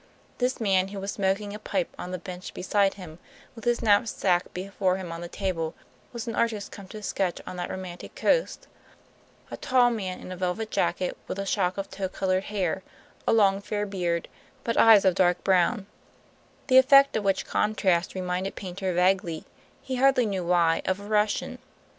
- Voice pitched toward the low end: No, high, 195 Hz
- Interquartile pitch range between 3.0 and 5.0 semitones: No, narrow, 2.6 semitones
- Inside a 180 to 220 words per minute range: Yes, average, 185 wpm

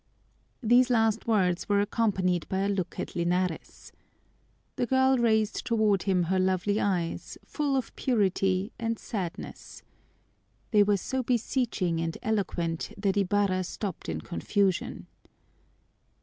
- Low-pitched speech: No, high, 200 Hz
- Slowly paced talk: Yes, slow, 125 wpm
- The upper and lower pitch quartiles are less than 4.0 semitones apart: Yes, average, 3.6 semitones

